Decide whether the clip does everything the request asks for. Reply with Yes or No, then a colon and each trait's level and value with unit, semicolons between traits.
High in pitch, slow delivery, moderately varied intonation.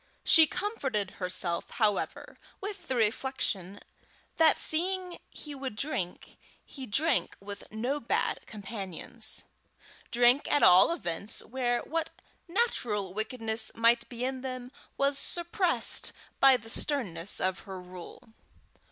No: high, 245 Hz; slow, 120 wpm; wide, 6.1 semitones